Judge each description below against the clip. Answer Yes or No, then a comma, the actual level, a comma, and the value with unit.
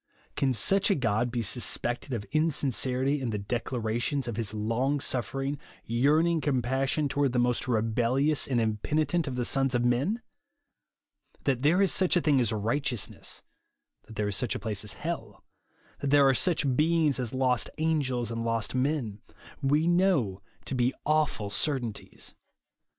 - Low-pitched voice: Yes, low, 130 Hz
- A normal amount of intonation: Yes, average, 4.1 semitones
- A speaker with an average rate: Yes, average, 160 wpm